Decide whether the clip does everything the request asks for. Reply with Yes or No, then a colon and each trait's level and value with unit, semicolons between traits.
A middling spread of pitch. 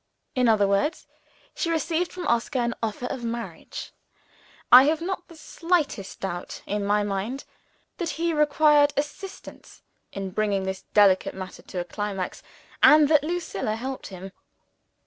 No: wide, 7.6 semitones